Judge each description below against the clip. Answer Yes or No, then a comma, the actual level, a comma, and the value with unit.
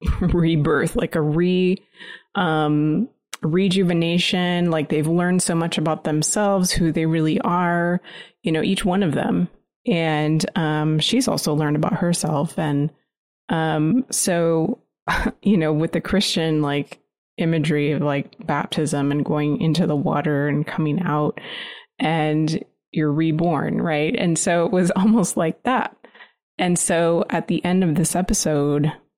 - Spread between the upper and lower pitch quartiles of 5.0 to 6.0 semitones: No, average, 3.0 semitones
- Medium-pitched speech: Yes, medium, 165 Hz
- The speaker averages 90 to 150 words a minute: Yes, average, 145 wpm